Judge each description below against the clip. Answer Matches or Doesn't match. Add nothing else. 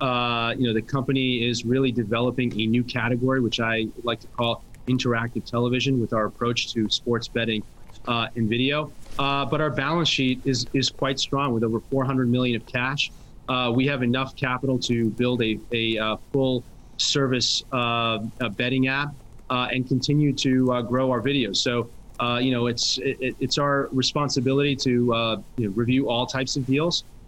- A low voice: Matches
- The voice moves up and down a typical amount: Doesn't match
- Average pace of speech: Matches